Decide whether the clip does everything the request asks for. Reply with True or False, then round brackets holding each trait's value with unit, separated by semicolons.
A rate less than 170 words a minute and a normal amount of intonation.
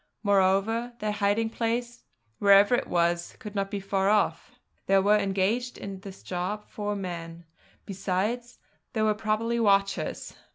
False (140 wpm; 2.3 semitones)